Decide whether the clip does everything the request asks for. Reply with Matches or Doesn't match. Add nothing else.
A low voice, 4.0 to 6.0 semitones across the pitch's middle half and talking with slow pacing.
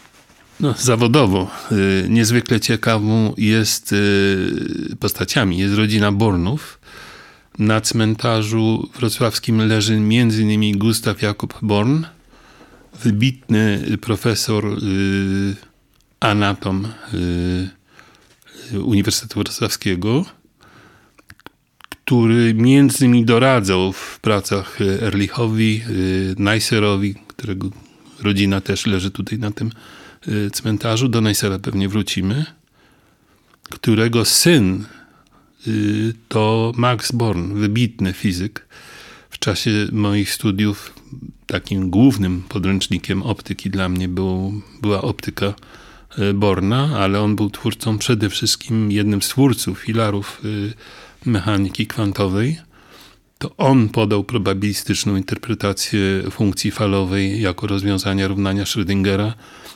Doesn't match